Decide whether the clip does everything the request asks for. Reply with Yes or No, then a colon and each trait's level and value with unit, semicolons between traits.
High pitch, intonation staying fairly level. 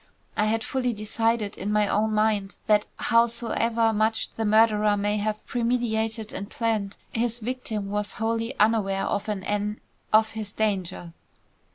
Yes: high, 215 Hz; narrow, 1.6 semitones